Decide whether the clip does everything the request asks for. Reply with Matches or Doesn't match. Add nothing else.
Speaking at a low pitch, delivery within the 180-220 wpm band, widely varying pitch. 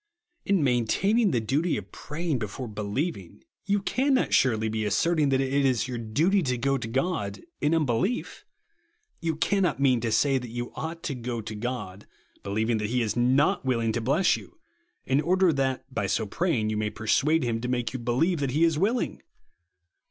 Matches